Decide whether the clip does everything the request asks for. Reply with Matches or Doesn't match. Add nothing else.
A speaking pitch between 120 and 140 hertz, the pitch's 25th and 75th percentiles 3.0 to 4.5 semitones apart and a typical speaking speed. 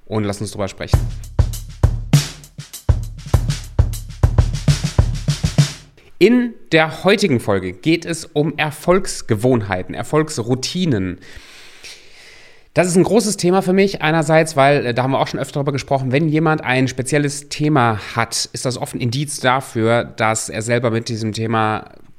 Doesn't match